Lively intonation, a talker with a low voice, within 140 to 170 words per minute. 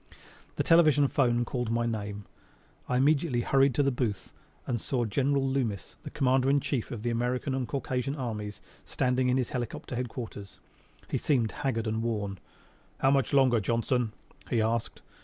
No: average, 2.9 semitones; low, 125 Hz; average, 165 wpm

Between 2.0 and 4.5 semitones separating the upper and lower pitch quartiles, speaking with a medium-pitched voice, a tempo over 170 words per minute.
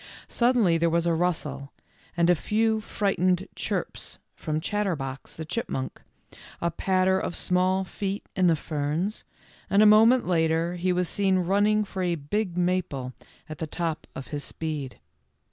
No: average, 3.4 semitones; medium, 180 Hz; average, 155 wpm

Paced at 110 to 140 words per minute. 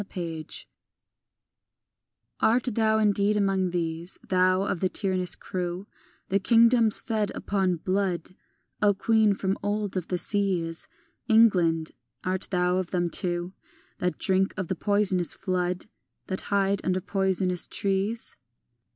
Yes: slow, 135 wpm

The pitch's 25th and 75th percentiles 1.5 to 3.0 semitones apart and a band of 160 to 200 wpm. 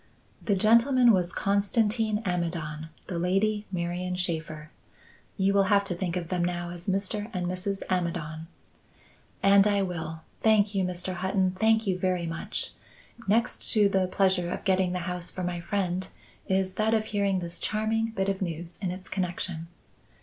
Yes: narrow, 2.5 semitones; average, 165 wpm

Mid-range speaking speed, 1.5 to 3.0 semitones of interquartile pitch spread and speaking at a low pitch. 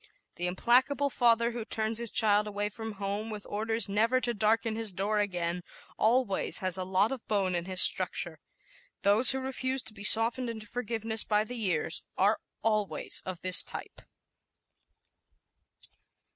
No: average, 160 wpm; average, 2.7 semitones; high, 215 Hz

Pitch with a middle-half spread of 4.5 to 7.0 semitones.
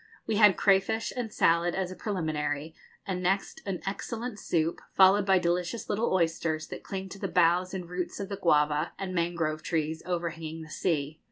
No: average, 3.1 semitones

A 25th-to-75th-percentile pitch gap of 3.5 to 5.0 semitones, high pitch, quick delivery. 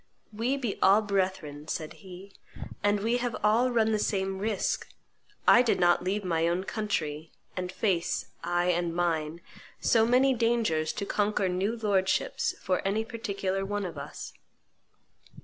No: average, 3.9 semitones; high, 195 Hz; average, 155 wpm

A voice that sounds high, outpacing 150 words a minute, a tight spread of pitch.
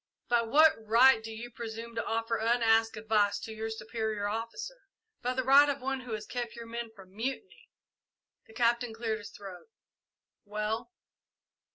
Yes: high, 230 Hz; average, 165 wpm; narrow, 1.8 semitones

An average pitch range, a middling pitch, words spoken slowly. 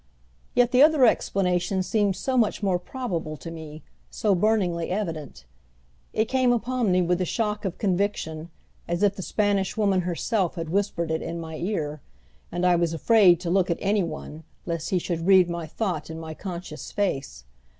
No: average, 3.8 semitones; medium, 180 Hz; average, 180 wpm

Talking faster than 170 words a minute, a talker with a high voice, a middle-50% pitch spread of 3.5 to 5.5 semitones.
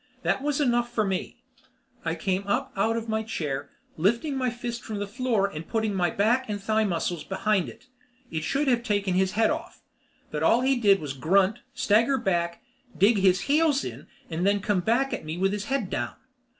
Yes: fast, 205 wpm; high, 210 Hz; average, 4.3 semitones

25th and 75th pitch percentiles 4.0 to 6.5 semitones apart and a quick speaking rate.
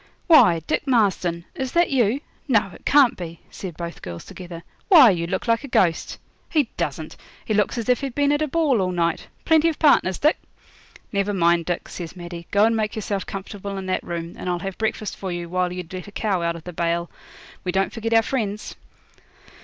Yes: average, 5.3 semitones; fast, 215 wpm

